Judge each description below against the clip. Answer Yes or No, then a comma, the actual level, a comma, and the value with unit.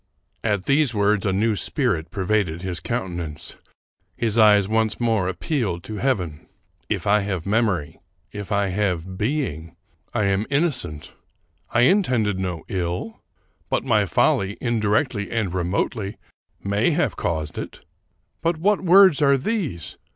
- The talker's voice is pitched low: Yes, low, 105 Hz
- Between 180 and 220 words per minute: No, average, 150 wpm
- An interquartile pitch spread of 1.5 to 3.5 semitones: No, average, 4.6 semitones